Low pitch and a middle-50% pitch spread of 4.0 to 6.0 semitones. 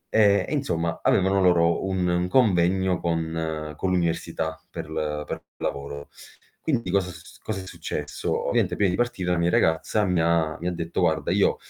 No: very low, 85 Hz; average, 2.7 semitones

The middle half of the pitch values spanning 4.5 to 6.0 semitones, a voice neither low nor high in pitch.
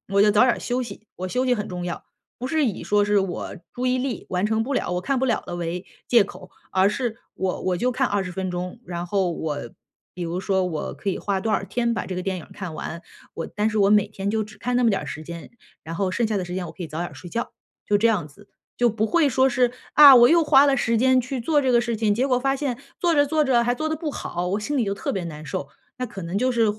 No: average, 5.3 semitones; high, 215 Hz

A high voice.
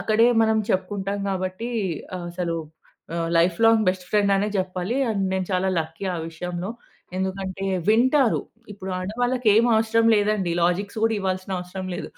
Yes: high, 195 Hz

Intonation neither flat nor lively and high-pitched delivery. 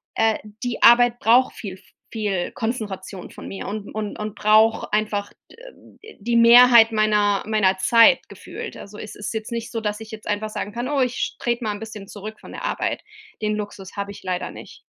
No: narrow, 2.2 semitones; high, 215 Hz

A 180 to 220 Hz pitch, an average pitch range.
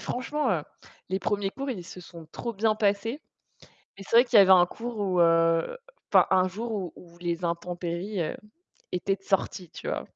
Yes: high, 190 Hz; average, 4.0 semitones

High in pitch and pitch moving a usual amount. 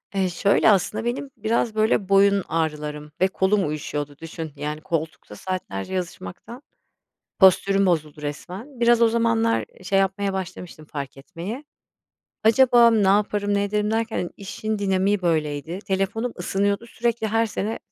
Yes: high, 195 Hz; average, 4.9 semitones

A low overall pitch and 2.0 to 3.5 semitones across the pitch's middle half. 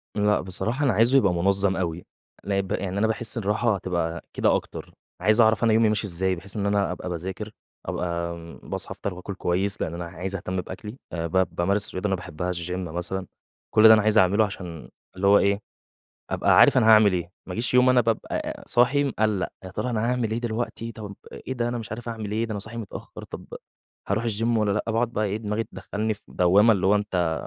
Yes: low, 100 Hz; average, 3.2 semitones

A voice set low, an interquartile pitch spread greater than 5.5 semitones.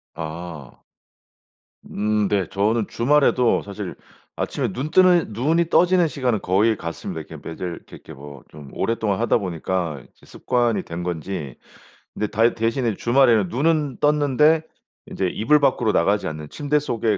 Yes: low, 110 Hz; wide, 6.9 semitones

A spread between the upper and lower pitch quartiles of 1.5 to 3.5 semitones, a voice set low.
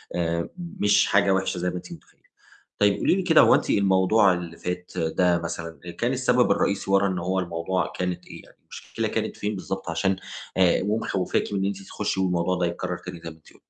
Yes: narrow, 2.4 semitones; very low, 95 Hz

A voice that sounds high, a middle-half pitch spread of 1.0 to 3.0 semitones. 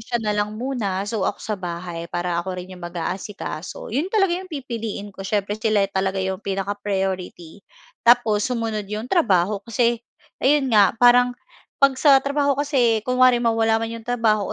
No: high, 215 Hz; average, 4.1 semitones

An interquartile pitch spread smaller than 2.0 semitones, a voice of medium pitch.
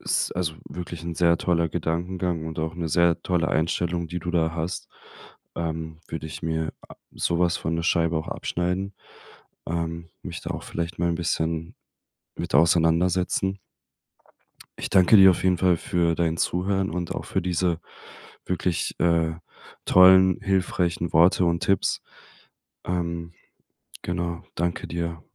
No: narrow, 1.4 semitones; very low, 85 Hz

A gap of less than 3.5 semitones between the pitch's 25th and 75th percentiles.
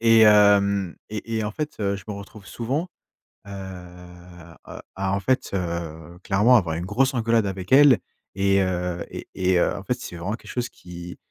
No: average, 3.9 semitones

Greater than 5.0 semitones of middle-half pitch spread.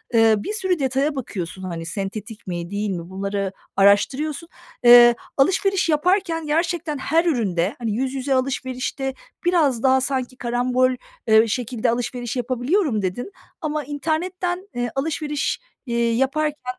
Yes: wide, 5.4 semitones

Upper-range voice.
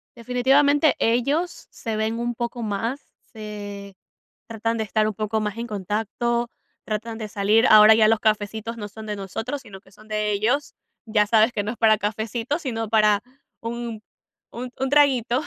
Yes: high, 220 Hz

